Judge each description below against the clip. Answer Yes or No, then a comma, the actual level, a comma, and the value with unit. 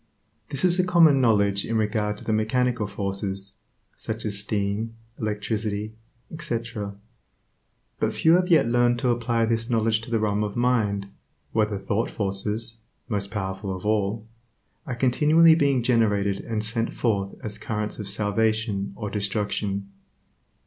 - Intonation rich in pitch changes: No, narrow, 2.6 semitones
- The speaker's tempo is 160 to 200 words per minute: No, average, 150 wpm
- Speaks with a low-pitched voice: Yes, low, 110 Hz